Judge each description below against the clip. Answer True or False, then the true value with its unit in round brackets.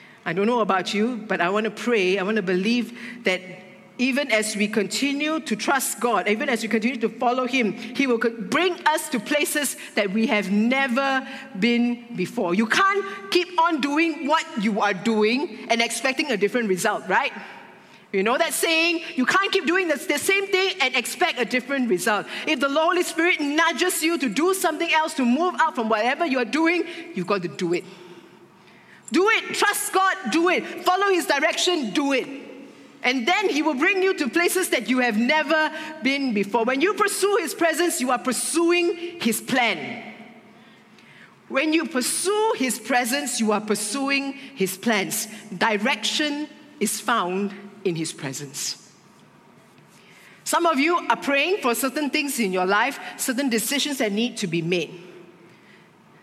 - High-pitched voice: True (255 Hz)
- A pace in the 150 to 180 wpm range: True (175 wpm)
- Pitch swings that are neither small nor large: False (6.7 semitones)